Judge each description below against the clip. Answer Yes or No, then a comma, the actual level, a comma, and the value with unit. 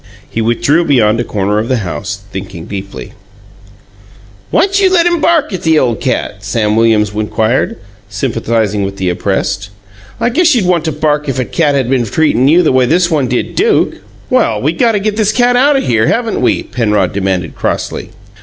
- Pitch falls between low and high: No, low, 125 Hz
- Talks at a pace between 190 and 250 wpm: Yes, average, 195 wpm